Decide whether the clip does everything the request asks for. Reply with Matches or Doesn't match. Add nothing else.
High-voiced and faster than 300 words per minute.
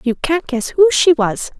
Doesn't match